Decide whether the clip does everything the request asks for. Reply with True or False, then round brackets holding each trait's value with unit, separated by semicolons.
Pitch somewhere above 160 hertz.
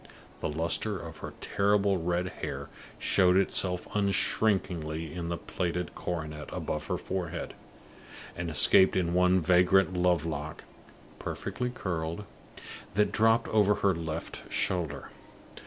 False (90 Hz)